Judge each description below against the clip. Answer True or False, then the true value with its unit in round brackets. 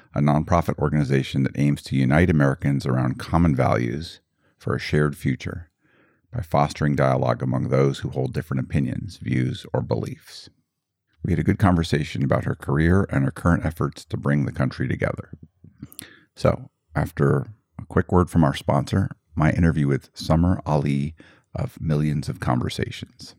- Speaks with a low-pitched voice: True (75 Hz)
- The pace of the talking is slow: False (155 wpm)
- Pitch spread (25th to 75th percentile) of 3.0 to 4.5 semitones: True (3.9 semitones)